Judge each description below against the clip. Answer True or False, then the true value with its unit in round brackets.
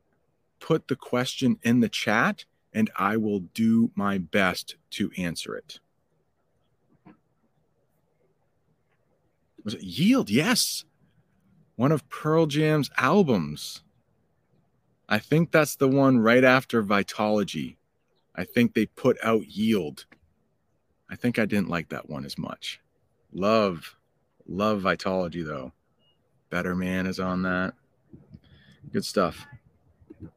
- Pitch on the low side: True (110 Hz)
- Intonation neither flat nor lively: False (8.3 semitones)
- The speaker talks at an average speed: False (115 wpm)